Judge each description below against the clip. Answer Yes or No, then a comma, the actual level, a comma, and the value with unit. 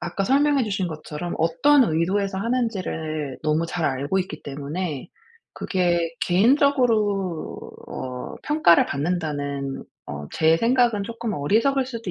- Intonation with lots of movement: Yes, wide, 6.8 semitones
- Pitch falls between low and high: Yes, medium, 180 Hz